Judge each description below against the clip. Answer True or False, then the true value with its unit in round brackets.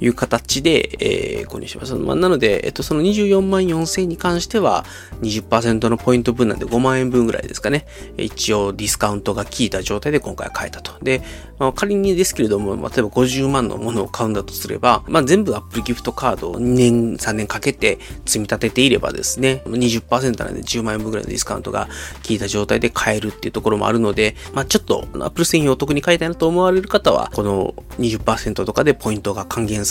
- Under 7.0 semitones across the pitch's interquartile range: True (5.3 semitones)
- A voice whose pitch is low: True (120 Hz)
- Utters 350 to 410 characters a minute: False (420 characters per minute)